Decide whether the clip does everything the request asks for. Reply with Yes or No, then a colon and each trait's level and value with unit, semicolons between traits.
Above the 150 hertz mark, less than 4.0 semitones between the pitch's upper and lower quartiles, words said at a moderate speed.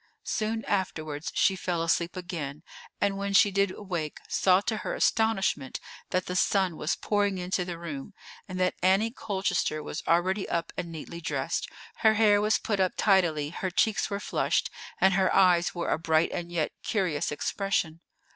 Yes: medium, 185 Hz; average, 3.1 semitones; average, 175 wpm